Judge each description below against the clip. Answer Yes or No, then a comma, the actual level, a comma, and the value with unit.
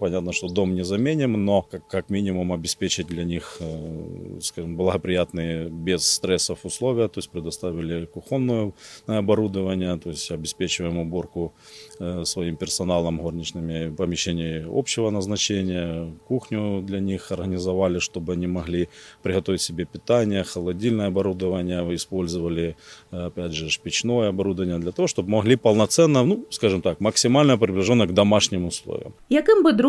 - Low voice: Yes, very low, 90 Hz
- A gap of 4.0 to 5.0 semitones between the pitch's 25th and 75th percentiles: No, average, 3.3 semitones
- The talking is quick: No, average, 120 wpm